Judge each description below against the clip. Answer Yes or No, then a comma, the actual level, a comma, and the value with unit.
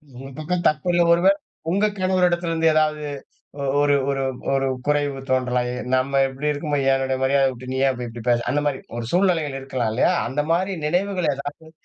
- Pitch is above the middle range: No, medium, 145 Hz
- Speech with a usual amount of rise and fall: Yes, average, 4.1 semitones